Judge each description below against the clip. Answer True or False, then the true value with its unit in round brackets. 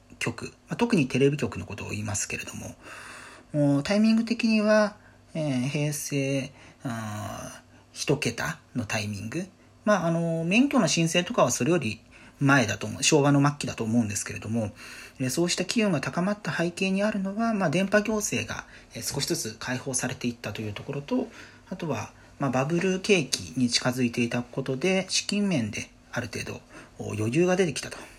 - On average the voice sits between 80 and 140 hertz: True (135 Hz)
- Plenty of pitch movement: True (7.1 semitones)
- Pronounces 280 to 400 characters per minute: True (315 characters per minute)